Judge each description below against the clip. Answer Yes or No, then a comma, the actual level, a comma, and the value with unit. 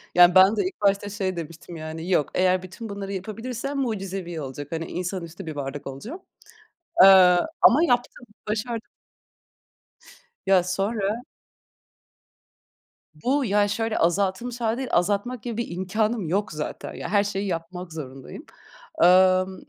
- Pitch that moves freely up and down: No, average, 4.2 semitones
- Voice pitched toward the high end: Yes, high, 195 Hz